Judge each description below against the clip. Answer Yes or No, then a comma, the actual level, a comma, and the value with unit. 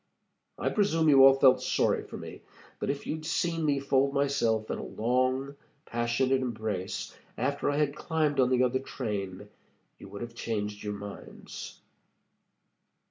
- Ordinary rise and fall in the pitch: Yes, average, 4.3 semitones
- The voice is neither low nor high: No, low, 130 Hz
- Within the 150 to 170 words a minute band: Yes, average, 155 wpm